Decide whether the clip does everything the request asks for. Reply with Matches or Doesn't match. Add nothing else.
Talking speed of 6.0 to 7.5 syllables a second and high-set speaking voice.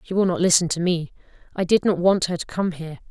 Doesn't match